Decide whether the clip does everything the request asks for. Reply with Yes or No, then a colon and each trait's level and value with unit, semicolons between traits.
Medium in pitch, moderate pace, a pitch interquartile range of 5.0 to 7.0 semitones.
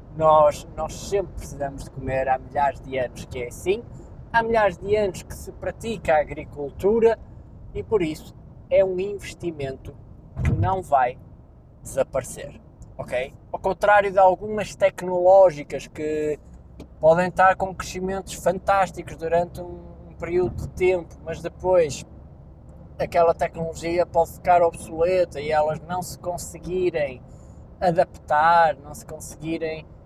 No: medium, 170 Hz; average, 130 wpm; average, 4.1 semitones